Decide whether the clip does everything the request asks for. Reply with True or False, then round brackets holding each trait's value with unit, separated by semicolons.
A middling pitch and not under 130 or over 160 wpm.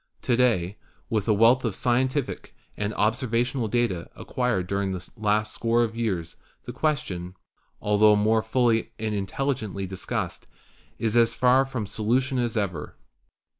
False (110 Hz; 145 wpm)